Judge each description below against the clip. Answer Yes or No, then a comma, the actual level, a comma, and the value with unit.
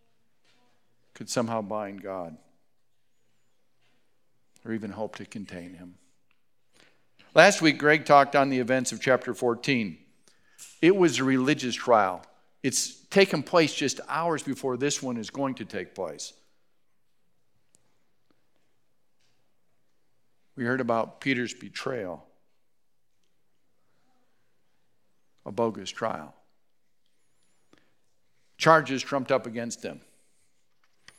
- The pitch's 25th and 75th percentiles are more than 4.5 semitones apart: No, average, 4.2 semitones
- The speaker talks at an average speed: No, slow, 100 wpm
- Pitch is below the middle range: Yes, low, 130 Hz